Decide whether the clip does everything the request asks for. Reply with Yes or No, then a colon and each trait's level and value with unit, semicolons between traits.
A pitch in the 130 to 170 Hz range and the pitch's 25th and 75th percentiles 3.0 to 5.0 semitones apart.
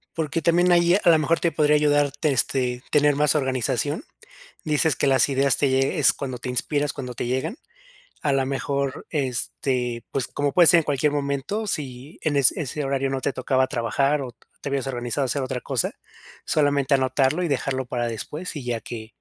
No: medium, 140 Hz; narrow, 2.4 semitones